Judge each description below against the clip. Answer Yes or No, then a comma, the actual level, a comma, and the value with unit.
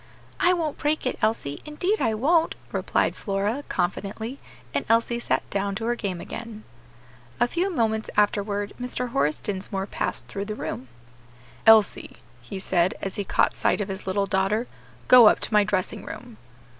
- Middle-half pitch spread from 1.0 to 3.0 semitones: No, average, 3.5 semitones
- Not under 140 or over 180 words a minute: Yes, average, 170 wpm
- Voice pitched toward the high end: Yes, high, 215 Hz